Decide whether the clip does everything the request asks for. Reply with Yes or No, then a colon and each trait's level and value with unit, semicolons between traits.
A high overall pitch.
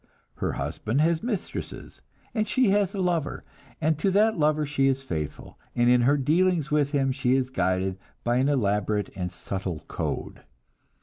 No: medium, 140 Hz